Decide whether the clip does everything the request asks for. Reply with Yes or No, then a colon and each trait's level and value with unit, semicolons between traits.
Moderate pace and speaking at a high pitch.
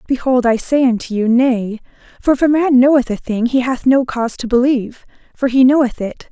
No: fast, 220 wpm; very high, 250 Hz